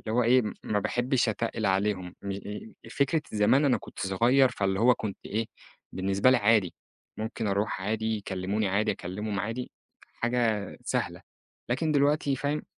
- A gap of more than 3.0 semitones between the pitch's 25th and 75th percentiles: Yes, average, 3.7 semitones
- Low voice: Yes, low, 110 Hz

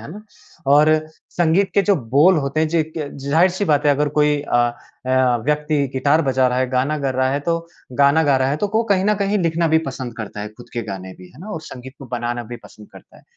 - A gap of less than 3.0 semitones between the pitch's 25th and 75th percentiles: No, average, 4.0 semitones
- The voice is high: No, medium, 145 Hz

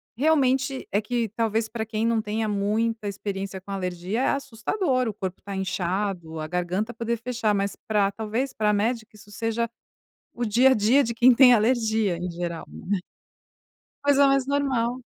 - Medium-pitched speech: No, high, 220 Hz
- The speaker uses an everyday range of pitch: Yes, average, 3.4 semitones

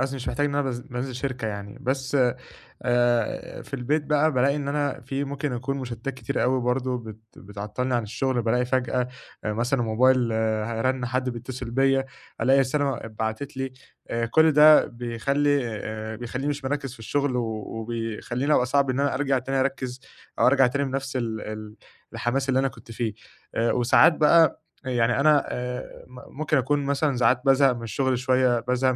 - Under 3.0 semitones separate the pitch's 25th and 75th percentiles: Yes, narrow, 2.6 semitones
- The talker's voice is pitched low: Yes, low, 130 Hz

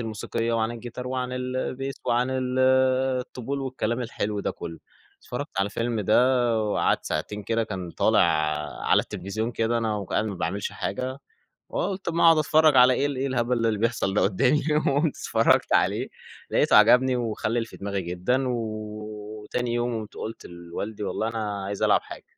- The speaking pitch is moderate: No, low, 115 Hz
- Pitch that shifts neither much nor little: Yes, average, 3.5 semitones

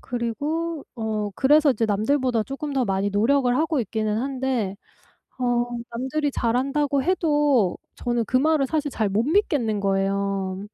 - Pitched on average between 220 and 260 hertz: Yes, very high, 250 Hz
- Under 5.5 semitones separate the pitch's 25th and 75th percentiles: Yes, average, 5.1 semitones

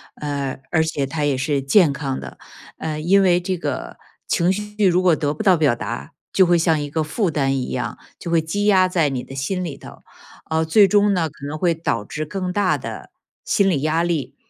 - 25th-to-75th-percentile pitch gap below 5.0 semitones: Yes, average, 4.2 semitones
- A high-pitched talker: No, medium, 160 Hz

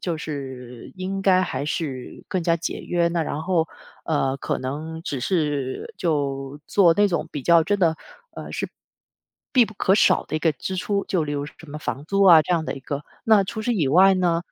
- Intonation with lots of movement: No, average, 4.4 semitones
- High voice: No, medium, 165 Hz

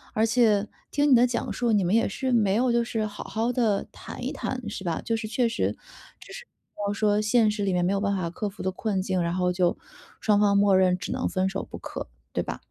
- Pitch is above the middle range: Yes, high, 210 Hz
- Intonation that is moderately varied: Yes, average, 3.3 semitones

